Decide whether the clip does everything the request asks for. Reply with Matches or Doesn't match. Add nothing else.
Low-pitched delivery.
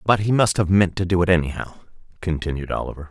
Matches